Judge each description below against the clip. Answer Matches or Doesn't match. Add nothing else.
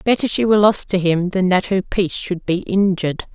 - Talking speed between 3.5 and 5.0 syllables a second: Doesn't match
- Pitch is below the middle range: Doesn't match